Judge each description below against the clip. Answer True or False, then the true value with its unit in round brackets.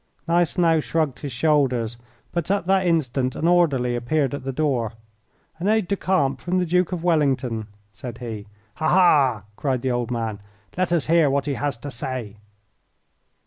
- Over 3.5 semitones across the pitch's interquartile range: True (5.6 semitones)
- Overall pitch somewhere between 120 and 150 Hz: True (140 Hz)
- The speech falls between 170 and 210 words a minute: True (175 wpm)